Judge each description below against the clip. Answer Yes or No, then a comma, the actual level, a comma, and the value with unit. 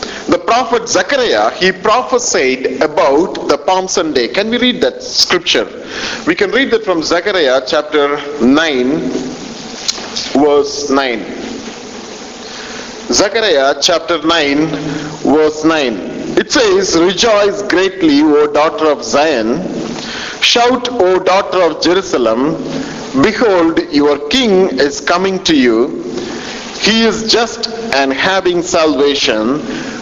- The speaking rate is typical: No, slow, 110 wpm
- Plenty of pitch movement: Yes, wide, 8.1 semitones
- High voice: Yes, high, 195 Hz